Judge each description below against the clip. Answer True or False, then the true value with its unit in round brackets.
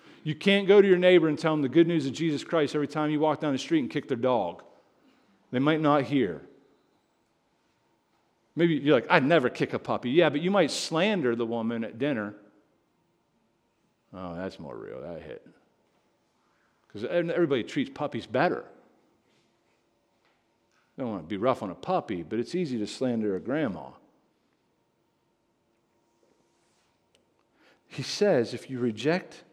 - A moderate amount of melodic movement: False (5.8 semitones)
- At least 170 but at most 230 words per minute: False (160 wpm)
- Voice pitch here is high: False (140 Hz)